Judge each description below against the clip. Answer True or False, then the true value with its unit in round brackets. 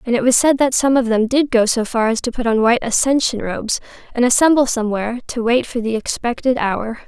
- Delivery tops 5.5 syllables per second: True (6.0 syllables/s)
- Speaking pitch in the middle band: False (240 Hz)